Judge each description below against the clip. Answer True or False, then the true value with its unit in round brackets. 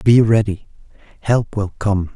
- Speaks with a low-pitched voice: True (105 Hz)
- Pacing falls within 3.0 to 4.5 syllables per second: True (4.0 syllables/s)